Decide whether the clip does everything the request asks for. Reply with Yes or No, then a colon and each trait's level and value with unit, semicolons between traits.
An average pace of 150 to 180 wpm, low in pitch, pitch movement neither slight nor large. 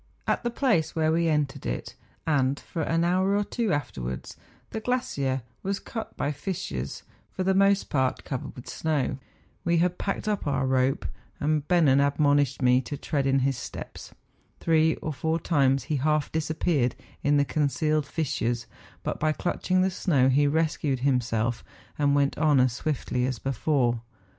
No: average, 165 wpm; medium, 145 Hz; average, 3.8 semitones